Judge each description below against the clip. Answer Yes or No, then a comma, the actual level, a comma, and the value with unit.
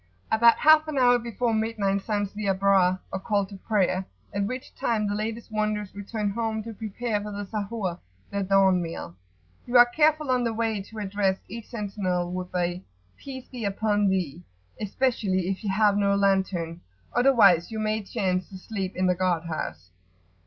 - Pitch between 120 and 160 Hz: No, high, 205 Hz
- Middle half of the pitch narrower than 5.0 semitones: Yes, average, 3.0 semitones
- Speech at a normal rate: Yes, average, 180 wpm